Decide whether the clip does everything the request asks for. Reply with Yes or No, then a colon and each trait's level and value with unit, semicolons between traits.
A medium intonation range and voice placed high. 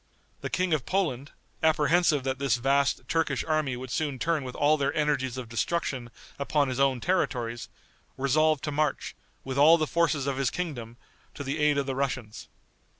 No: average, 3.0 semitones; medium, 140 Hz